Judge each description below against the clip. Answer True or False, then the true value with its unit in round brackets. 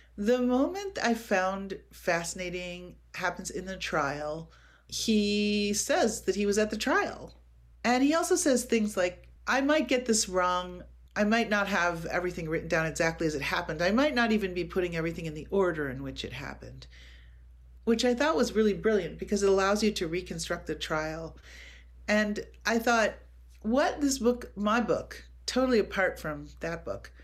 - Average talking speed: True (175 wpm)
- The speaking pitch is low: False (190 Hz)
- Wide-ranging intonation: True (5.8 semitones)